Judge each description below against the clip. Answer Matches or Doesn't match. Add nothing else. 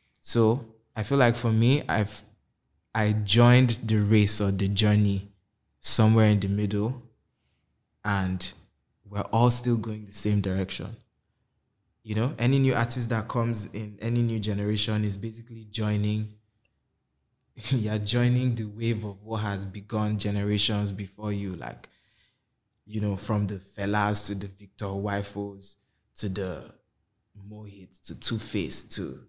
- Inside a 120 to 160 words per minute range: Matches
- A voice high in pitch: Doesn't match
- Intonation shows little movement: Matches